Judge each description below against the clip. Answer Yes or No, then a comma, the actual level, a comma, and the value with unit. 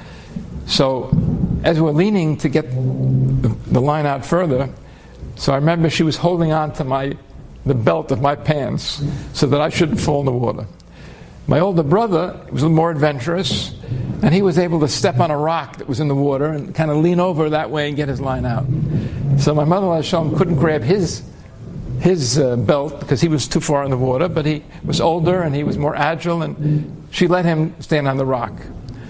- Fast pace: Yes, fast, 210 wpm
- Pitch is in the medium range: Yes, medium, 150 Hz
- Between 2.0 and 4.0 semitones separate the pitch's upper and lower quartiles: Yes, average, 3.3 semitones